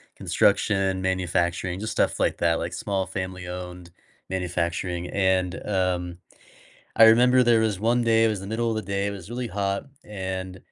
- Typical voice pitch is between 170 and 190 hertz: No, very low, 95 Hz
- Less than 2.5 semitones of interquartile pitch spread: No, average, 2.9 semitones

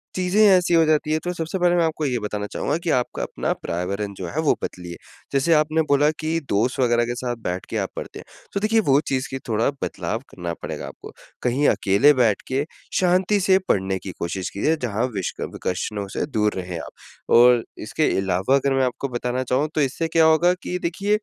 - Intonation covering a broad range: Yes, wide, 7.4 semitones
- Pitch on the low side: Yes, low, 130 Hz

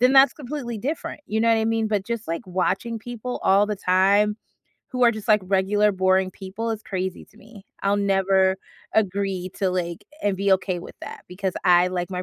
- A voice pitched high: Yes, high, 200 Hz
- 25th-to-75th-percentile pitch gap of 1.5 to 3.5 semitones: Yes, average, 2.9 semitones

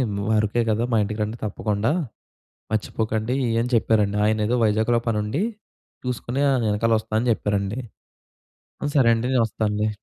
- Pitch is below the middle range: Yes, low, 110 Hz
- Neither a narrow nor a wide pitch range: No, narrow, 2.0 semitones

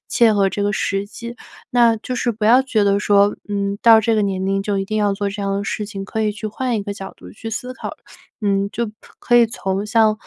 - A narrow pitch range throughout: Yes, narrow, 2.3 semitones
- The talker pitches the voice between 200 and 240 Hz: Yes, high, 210 Hz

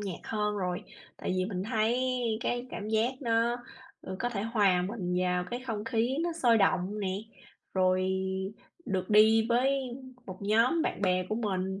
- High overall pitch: Yes, high, 215 Hz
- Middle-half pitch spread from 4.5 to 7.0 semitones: No, average, 4.0 semitones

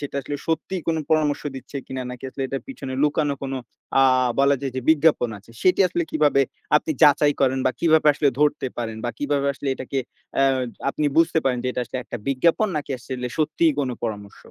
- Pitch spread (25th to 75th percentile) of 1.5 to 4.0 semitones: Yes, average, 2.9 semitones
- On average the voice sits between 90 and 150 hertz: Yes, medium, 140 Hz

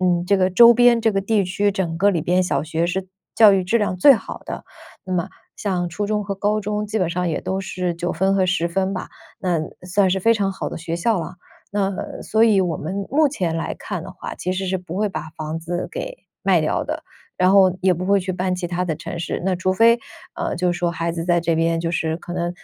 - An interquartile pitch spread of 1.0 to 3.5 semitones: Yes, narrow, 2.6 semitones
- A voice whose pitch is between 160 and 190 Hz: Yes, medium, 185 Hz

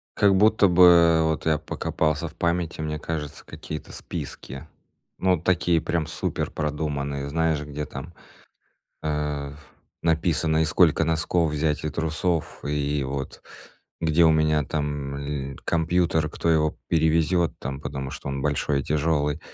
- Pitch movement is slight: Yes, narrow, 2.1 semitones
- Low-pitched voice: Yes, very low, 80 Hz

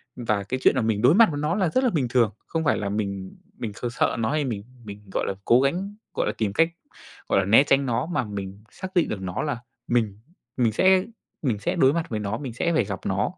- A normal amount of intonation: No, wide, 6.7 semitones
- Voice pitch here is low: Yes, low, 120 Hz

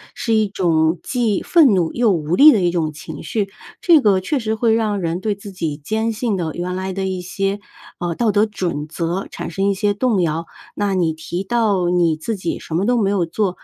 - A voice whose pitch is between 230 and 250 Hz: No, high, 195 Hz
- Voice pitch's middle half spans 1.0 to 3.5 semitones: No, average, 4.0 semitones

